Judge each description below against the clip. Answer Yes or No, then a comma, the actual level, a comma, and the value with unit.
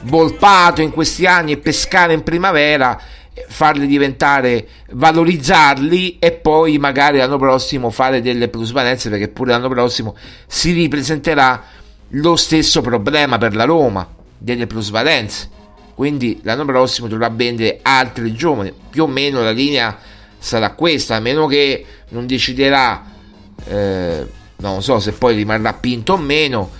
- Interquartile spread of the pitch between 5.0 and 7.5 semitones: Yes, wide, 5.5 semitones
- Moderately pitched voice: No, low, 130 Hz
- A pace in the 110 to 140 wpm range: Yes, average, 135 wpm